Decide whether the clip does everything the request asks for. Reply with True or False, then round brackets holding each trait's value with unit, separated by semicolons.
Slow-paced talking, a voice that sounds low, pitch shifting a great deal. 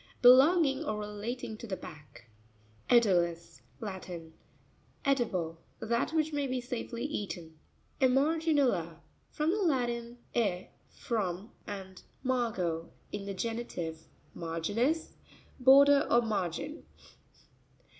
False (95 wpm; 230 Hz; 6.6 semitones)